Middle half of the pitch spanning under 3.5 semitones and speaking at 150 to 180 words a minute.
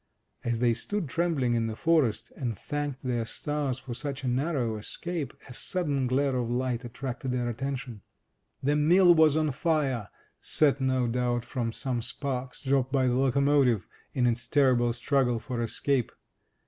Yes: average, 2.9 semitones; average, 160 wpm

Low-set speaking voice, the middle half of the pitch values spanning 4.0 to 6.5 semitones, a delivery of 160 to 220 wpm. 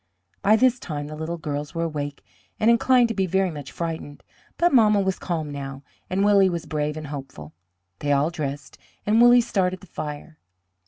No: medium, 165 Hz; wide, 5.5 semitones; average, 190 wpm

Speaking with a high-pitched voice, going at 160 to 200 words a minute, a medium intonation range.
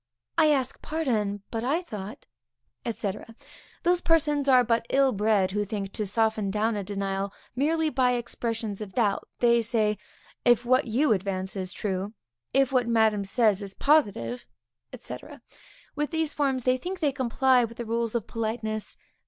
Yes: high, 230 Hz; average, 165 wpm; average, 4.2 semitones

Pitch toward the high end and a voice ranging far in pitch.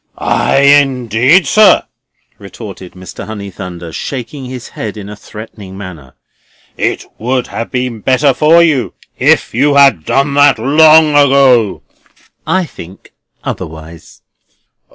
No: low, 125 Hz; wide, 6.0 semitones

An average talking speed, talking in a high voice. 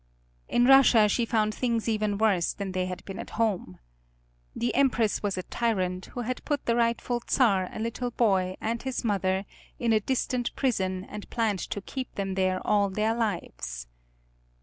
Yes: average, 175 wpm; high, 215 Hz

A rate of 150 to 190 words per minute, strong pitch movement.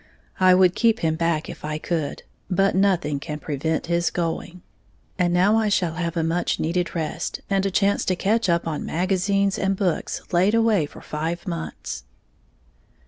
No: average, 175 wpm; average, 3.1 semitones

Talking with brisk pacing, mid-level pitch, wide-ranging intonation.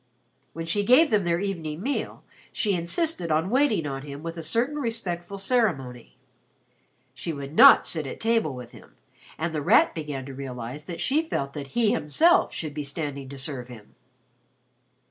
No: average, 175 wpm; medium, 165 Hz; wide, 7.1 semitones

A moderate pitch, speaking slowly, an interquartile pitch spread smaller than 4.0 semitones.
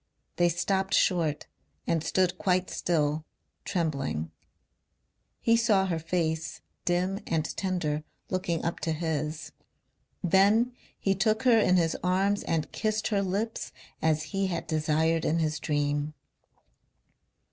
Yes: medium, 170 Hz; slow, 125 wpm; average, 3.5 semitones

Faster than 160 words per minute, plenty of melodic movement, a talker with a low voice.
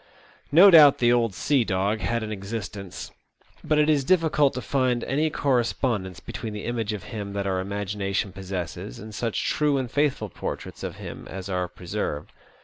Yes: average, 175 wpm; wide, 5.7 semitones; low, 110 Hz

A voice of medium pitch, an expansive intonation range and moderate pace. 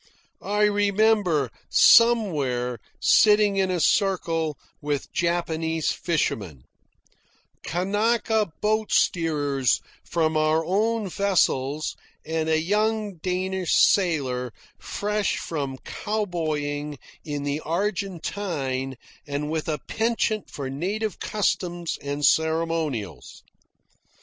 No: medium, 165 Hz; wide, 5.7 semitones; slow, 90 wpm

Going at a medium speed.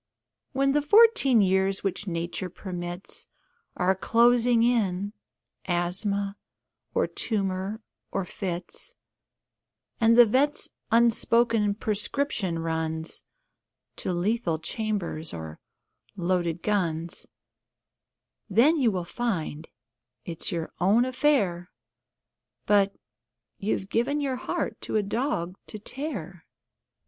No: slow, 95 wpm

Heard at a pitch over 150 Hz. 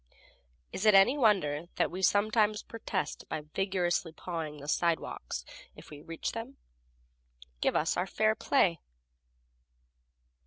Yes: medium, 185 Hz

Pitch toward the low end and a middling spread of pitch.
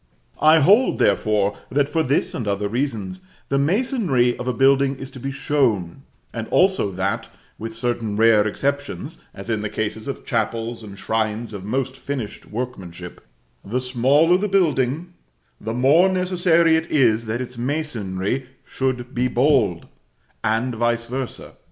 Yes: low, 125 Hz; average, 4.5 semitones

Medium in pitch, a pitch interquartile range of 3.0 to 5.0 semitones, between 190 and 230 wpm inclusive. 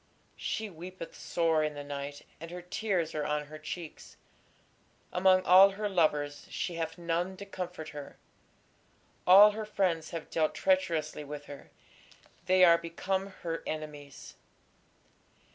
No: medium, 170 Hz; average, 3.4 semitones; average, 140 wpm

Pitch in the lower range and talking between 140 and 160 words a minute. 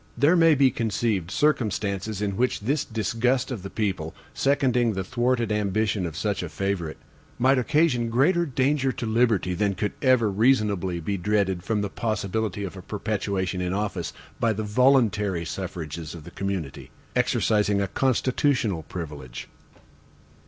Yes: low, 105 Hz; average, 150 wpm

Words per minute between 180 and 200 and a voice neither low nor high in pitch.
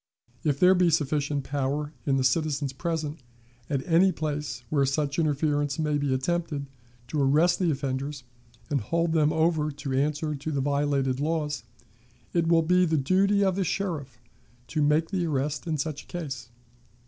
No: average, 165 wpm; medium, 150 Hz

